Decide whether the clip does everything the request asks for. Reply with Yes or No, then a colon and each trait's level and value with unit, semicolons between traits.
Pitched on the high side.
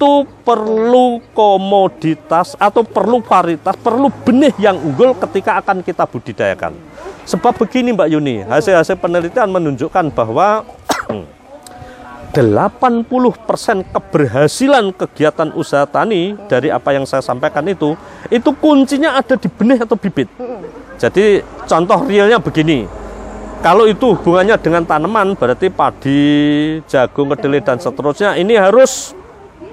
Yes: high, 195 Hz